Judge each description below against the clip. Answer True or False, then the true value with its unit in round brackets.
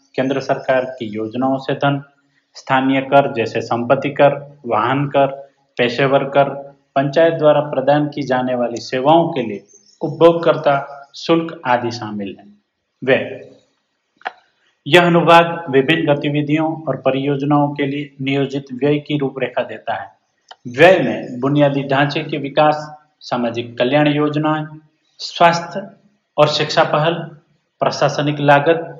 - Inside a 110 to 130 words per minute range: True (120 wpm)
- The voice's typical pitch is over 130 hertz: True (140 Hz)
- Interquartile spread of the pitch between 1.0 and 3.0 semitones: True (2.4 semitones)